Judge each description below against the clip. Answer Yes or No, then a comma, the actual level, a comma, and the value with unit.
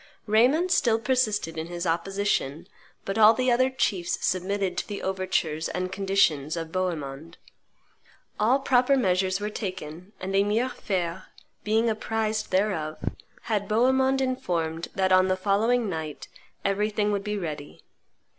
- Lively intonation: No, average, 4.1 semitones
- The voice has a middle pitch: No, high, 195 Hz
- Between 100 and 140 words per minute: Yes, slow, 135 wpm